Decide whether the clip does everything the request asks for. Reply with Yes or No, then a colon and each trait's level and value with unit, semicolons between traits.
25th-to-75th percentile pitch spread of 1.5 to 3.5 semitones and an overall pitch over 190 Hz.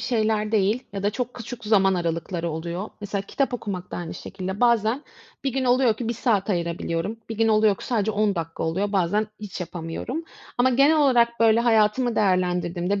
No: average, 4.3 semitones; high, 210 Hz